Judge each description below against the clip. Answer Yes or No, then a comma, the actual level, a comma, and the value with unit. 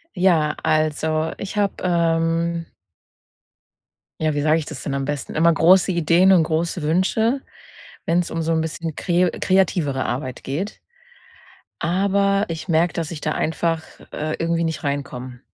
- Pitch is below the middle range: No, medium, 165 Hz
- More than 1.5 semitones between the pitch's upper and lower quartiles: Yes, narrow, 2.4 semitones